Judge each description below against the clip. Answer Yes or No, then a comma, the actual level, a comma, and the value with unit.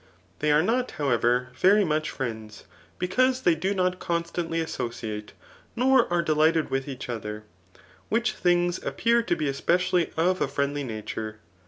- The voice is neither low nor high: Yes, medium, 160 Hz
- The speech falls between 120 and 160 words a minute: Yes, average, 150 wpm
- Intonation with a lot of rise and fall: Yes, wide, 6.2 semitones